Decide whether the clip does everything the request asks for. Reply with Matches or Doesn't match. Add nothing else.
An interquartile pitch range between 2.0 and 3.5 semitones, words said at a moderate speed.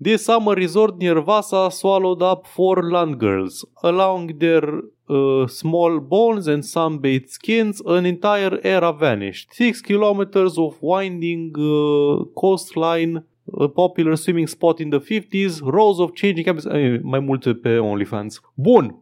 Doesn't match